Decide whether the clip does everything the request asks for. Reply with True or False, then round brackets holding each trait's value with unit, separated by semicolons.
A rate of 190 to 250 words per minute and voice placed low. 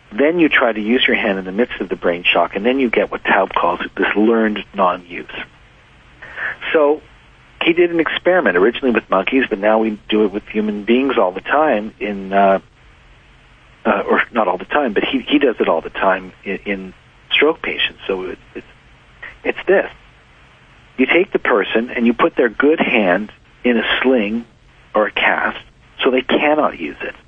True (200 wpm; 110 Hz)